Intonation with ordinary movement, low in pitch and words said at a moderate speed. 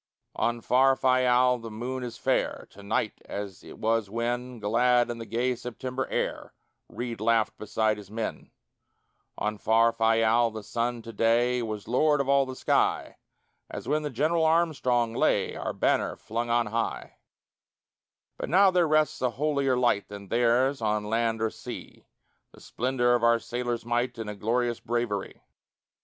No: narrow, 2.1 semitones; low, 120 Hz; average, 160 wpm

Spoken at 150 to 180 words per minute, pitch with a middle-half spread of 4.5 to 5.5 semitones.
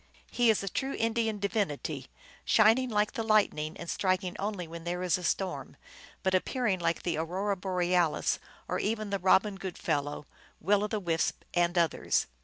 No: average, 175 wpm; average, 3.6 semitones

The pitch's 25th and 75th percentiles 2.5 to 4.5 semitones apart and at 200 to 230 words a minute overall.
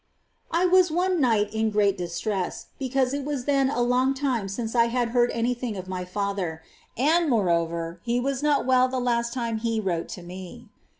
No: average, 4.9 semitones; fast, 205 wpm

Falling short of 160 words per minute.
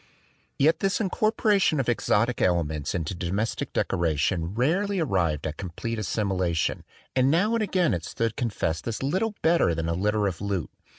No: average, 165 wpm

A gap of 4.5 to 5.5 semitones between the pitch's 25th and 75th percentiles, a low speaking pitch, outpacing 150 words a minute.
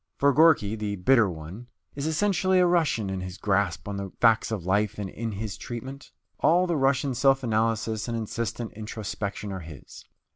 Yes: average, 5.1 semitones; low, 110 Hz; average, 180 wpm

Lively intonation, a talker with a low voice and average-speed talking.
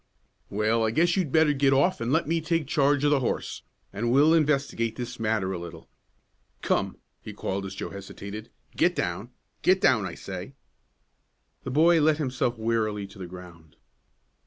Yes: wide, 6.9 semitones; low, 120 Hz; average, 175 wpm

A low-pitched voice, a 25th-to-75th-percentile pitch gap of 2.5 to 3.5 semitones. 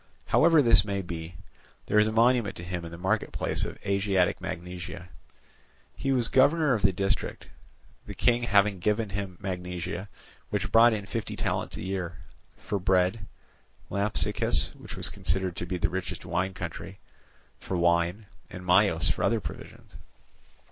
Yes: very low, 95 Hz; average, 3.1 semitones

